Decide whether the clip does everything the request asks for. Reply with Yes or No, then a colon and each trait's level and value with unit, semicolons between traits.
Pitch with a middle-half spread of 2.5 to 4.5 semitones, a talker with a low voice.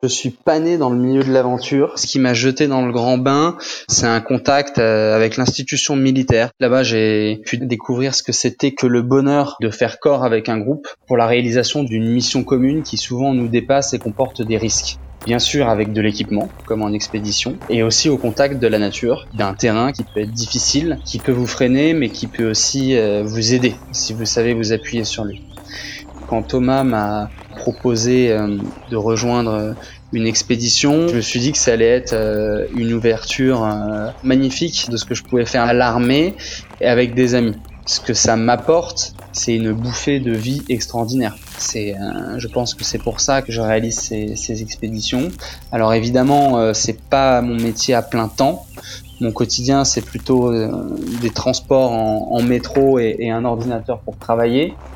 Yes: average, 2.8 semitones; low, 120 Hz